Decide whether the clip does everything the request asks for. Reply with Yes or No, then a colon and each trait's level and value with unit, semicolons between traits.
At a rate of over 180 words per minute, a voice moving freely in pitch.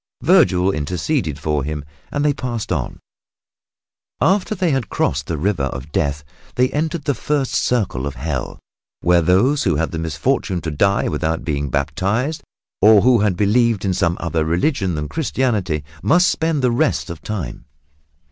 No: average, 165 wpm; wide, 8.7 semitones